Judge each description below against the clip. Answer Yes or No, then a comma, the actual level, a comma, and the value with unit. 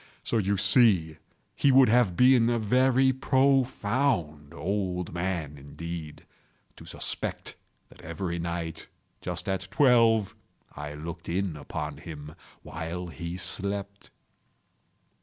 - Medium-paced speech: No, slow, 115 wpm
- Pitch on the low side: Yes, very low, 90 Hz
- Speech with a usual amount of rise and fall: No, wide, 5.9 semitones